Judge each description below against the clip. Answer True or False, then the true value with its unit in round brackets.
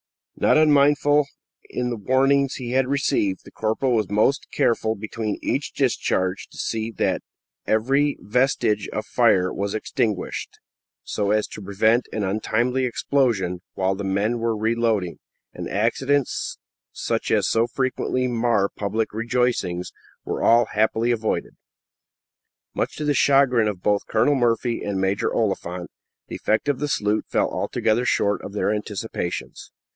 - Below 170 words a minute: True (145 wpm)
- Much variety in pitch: False (3.7 semitones)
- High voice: False (115 Hz)